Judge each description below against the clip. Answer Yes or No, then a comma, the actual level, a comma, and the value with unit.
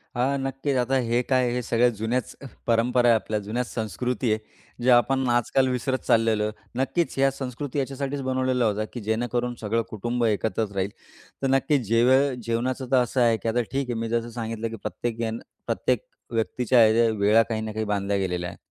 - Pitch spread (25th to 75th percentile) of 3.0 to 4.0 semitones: No, narrow, 2.6 semitones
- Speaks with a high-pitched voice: No, low, 120 Hz